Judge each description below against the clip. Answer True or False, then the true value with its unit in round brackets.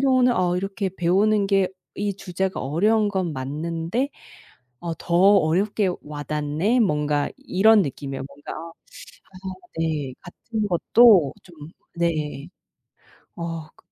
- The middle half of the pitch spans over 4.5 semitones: True (5.1 semitones)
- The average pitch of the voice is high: False (175 Hz)